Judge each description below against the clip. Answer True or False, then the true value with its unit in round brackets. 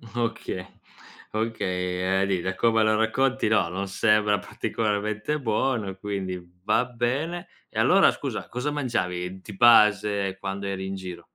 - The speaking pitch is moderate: False (105 Hz)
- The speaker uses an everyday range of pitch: True (3.4 semitones)